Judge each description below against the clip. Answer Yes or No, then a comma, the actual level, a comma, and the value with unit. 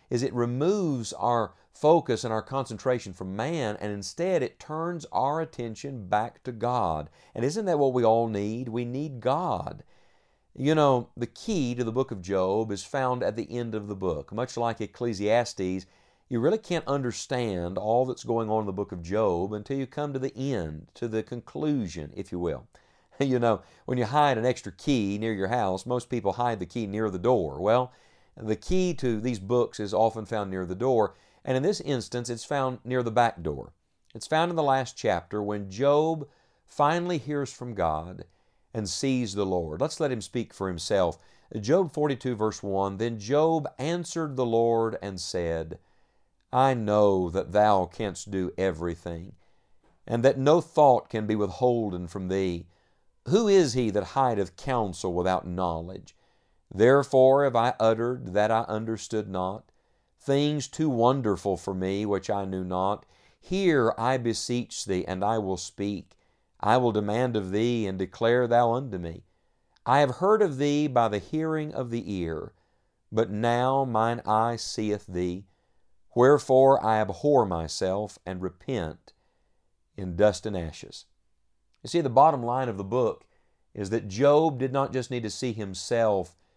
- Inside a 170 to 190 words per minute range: Yes, average, 175 wpm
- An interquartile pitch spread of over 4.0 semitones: Yes, average, 5.0 semitones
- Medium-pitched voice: No, low, 115 Hz